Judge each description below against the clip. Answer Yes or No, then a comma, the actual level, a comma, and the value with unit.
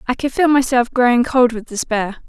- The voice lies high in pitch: Yes, high, 245 Hz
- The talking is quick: Yes, fast, 210 wpm